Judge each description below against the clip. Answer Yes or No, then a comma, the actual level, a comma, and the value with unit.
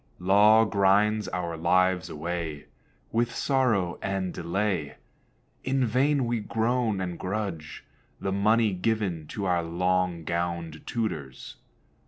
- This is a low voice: Yes, very low, 95 Hz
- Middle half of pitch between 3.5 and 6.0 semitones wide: Yes, average, 4.2 semitones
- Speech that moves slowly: Yes, slow, 115 wpm